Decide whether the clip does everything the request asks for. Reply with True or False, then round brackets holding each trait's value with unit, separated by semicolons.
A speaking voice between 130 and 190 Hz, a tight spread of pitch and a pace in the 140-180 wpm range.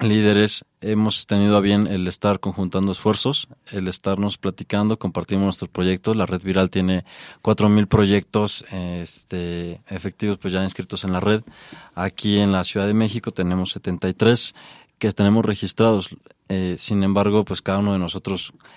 False (100 Hz; 2.2 semitones; 155 wpm)